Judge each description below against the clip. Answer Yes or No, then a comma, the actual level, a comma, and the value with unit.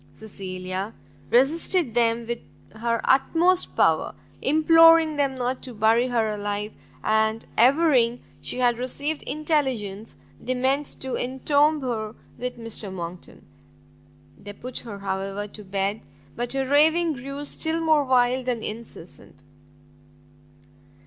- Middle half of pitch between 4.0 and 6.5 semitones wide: Yes, average, 4.8 semitones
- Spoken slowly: Yes, slow, 120 wpm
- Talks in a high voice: Yes, high, 245 Hz